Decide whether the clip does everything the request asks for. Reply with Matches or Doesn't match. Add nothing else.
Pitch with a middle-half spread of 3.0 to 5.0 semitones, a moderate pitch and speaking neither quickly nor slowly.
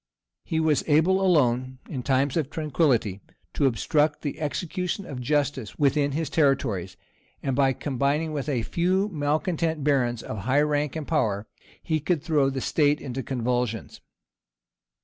Matches